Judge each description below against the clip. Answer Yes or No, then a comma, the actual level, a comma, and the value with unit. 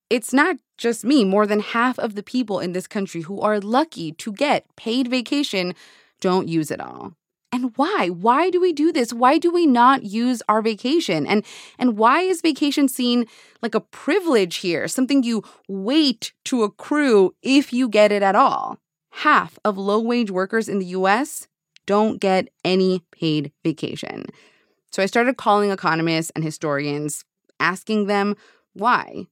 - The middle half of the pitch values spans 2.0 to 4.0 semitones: No, wide, 5.5 semitones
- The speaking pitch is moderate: No, high, 220 Hz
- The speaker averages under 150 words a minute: No, average, 170 wpm